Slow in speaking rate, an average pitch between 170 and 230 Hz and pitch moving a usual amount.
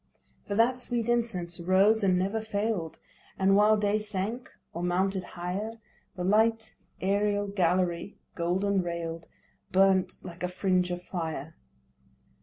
Yes: slow, 130 wpm; high, 190 Hz; average, 3.0 semitones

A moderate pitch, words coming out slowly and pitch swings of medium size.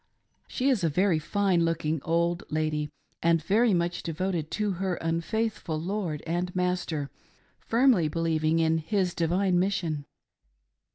Yes: medium, 170 Hz; slow, 130 wpm; average, 3.1 semitones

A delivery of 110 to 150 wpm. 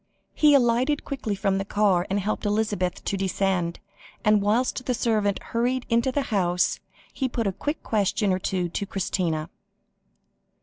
No: average, 160 wpm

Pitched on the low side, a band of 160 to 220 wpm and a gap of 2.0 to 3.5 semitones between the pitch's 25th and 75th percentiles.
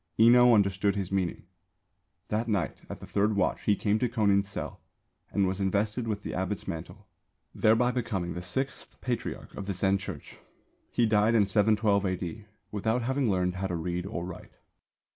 Yes: low, 100 Hz; average, 175 wpm; average, 2.8 semitones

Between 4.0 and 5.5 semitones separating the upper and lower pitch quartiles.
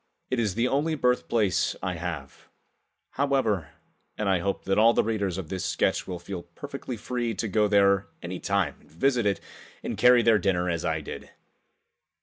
Yes: average, 4.7 semitones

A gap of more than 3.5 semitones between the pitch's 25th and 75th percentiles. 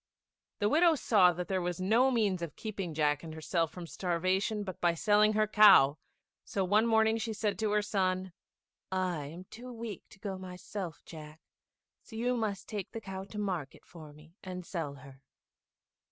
Yes: average, 4.0 semitones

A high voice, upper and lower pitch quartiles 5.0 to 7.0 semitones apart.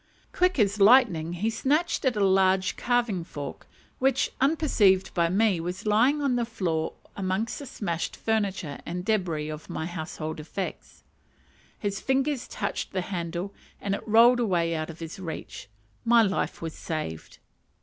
Yes: high, 195 Hz; wide, 5.5 semitones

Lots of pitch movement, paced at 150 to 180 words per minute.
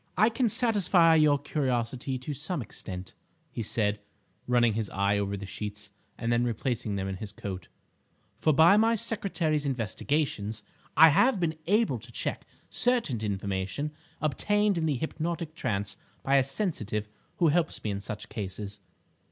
Yes: wide, 7.8 semitones; average, 155 wpm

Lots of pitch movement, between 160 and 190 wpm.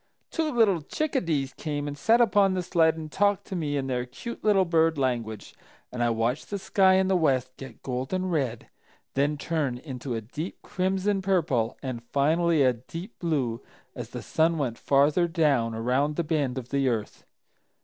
Yes: wide, 6.1 semitones; average, 180 wpm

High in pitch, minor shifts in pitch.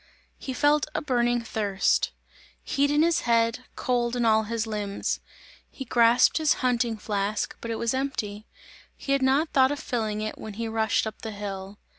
No: high, 230 Hz; average, 3.4 semitones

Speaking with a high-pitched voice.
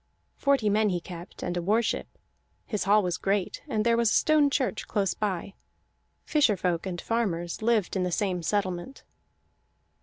Yes: high, 205 Hz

